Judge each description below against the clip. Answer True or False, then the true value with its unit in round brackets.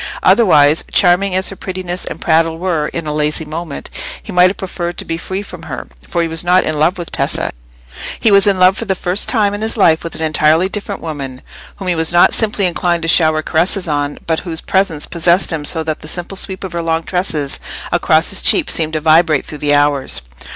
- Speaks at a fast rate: True (225 wpm)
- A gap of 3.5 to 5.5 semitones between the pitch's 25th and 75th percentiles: False (3.1 semitones)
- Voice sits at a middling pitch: True (170 Hz)